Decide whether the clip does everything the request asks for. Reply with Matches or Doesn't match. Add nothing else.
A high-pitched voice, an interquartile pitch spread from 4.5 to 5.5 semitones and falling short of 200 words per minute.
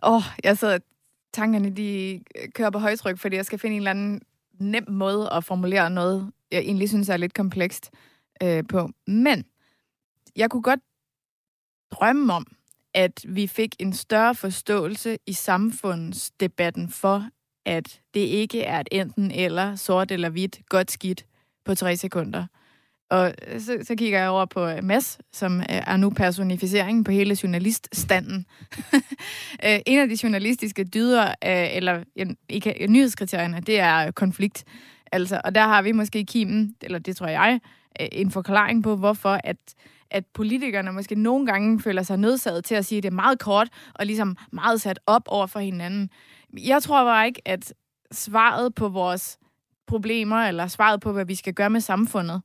Doesn't match